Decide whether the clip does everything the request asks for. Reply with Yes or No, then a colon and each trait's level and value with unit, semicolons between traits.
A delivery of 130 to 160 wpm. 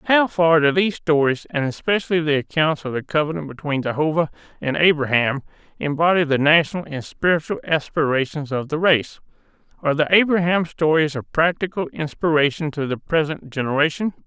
Yes: average, 150 wpm